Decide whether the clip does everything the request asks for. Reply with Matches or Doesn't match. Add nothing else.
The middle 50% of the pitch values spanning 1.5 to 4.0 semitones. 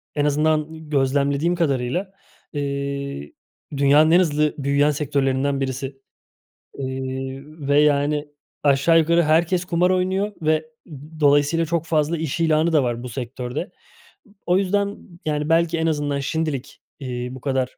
Matches